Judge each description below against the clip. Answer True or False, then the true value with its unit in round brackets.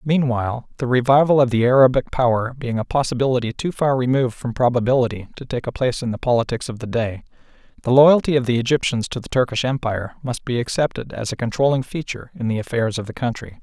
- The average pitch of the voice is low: True (125 Hz)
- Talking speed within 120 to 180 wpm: False (205 wpm)